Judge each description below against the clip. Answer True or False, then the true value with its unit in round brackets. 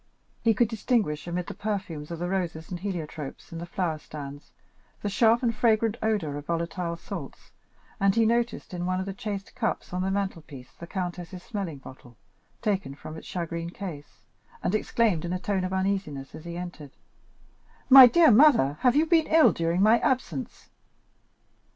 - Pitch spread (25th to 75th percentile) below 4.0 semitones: False (4.7 semitones)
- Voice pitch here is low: False (185 Hz)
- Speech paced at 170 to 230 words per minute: True (180 wpm)